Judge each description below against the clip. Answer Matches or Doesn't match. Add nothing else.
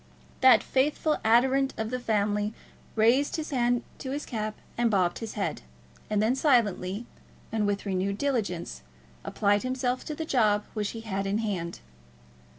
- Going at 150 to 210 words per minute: Matches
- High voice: Matches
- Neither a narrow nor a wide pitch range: Matches